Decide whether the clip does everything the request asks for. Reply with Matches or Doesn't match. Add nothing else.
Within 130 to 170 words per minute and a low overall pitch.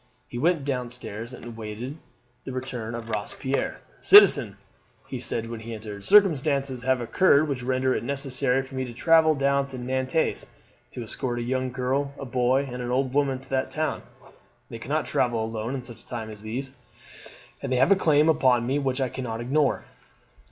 Doesn't match